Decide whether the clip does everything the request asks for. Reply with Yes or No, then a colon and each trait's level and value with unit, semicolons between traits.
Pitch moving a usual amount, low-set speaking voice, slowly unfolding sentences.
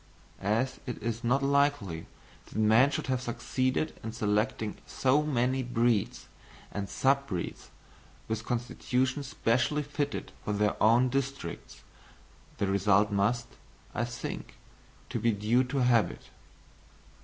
Yes: average, 3.6 semitones; low, 120 Hz; slow, 125 wpm